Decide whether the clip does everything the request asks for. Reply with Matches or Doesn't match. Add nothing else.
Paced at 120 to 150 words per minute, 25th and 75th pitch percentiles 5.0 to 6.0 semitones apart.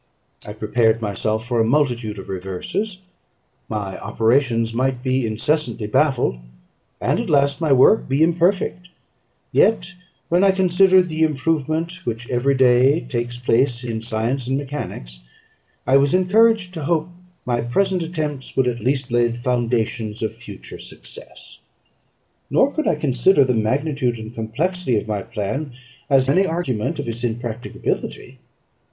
Matches